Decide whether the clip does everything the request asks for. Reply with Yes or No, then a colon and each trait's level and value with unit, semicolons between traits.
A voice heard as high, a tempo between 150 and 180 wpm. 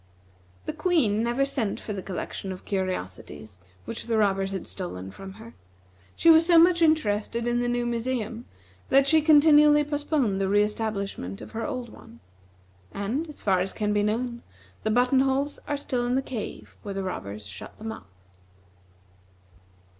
Yes: high, 230 Hz; average, 170 wpm